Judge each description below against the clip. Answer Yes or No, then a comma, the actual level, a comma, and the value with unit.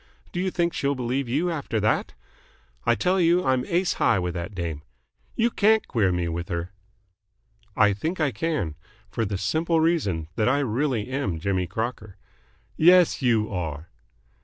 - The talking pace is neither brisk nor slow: Yes, average, 165 wpm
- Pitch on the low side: Yes, low, 120 Hz